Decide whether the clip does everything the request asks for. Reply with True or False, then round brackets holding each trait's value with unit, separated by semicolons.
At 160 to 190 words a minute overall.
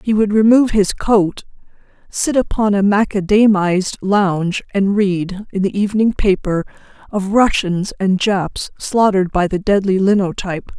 False (140 wpm)